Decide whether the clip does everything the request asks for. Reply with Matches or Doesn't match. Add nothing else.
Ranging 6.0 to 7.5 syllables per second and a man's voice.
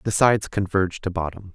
Matches